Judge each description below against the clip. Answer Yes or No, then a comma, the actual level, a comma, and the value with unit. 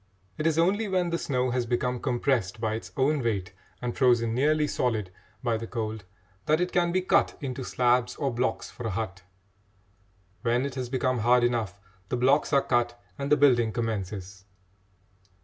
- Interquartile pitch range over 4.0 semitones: No, average, 3.5 semitones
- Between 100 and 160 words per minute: No, average, 180 wpm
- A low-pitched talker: Yes, low, 125 Hz